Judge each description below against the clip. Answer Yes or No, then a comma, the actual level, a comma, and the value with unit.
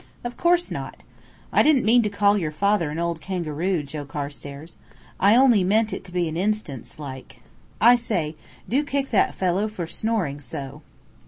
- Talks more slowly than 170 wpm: No, average, 175 wpm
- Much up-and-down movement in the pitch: Yes, wide, 6.3 semitones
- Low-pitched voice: No, medium, 185 Hz